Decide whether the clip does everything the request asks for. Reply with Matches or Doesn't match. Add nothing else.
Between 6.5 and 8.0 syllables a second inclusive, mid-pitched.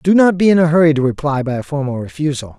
Matches